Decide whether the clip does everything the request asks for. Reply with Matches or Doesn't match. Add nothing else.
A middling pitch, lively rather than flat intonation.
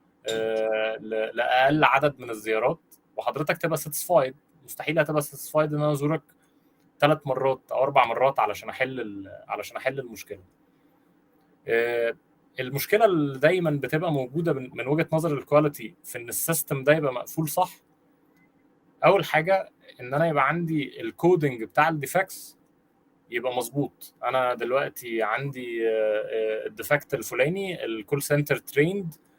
Doesn't match